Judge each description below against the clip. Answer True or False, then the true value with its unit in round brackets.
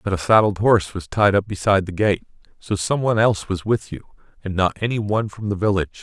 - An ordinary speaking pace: False (240 wpm)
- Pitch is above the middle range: False (100 Hz)